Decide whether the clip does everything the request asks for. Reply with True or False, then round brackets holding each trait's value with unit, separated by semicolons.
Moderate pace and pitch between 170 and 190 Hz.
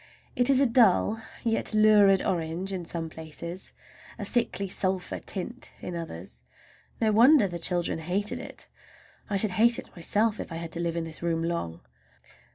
True (170 wpm; 185 Hz)